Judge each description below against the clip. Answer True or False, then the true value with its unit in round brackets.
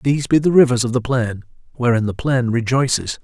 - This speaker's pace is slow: False (205 wpm)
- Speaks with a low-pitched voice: True (125 Hz)